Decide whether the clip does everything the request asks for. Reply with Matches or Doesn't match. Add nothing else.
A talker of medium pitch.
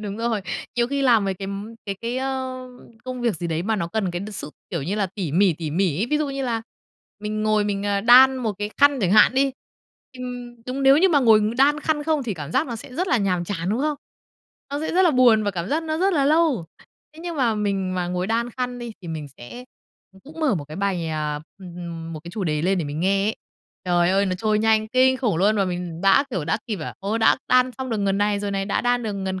Doesn't match